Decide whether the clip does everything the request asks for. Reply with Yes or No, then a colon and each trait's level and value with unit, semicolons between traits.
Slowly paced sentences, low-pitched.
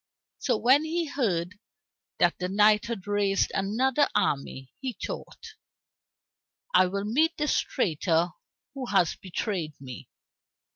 No: slow, 125 wpm; high, 205 Hz